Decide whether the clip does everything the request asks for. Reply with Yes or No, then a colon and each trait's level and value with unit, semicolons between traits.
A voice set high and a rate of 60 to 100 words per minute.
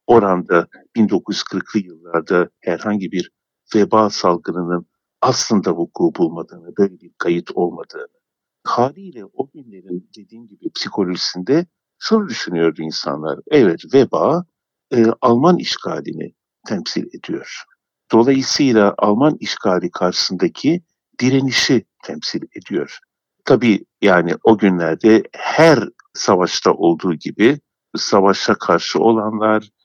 No: low, 110 Hz; slow, 95 wpm